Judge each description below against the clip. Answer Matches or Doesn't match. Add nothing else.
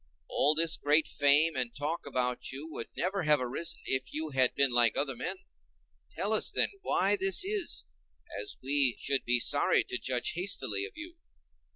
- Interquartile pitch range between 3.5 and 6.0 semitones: Matches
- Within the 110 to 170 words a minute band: Doesn't match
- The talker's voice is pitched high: Doesn't match